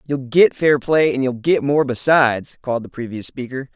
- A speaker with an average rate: No, fast, 210 wpm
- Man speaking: Yes, male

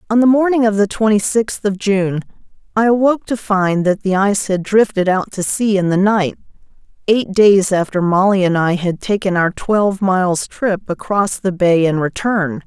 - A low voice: No, high, 195 Hz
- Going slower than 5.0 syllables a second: Yes, 4.8 syllables/s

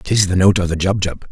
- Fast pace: Yes, fast, 275 wpm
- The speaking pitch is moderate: No, very low, 95 Hz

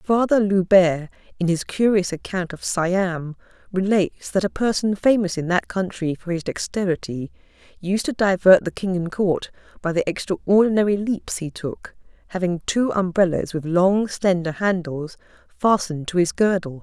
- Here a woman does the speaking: Yes, female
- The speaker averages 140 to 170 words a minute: Yes, average, 155 wpm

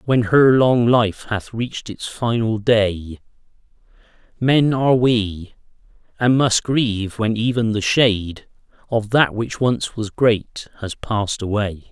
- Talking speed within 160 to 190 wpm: No, average, 140 wpm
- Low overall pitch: Yes, low, 110 Hz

